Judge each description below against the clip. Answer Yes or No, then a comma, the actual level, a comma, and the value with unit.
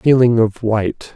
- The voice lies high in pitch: No, low, 115 Hz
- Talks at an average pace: Yes, average, 155 wpm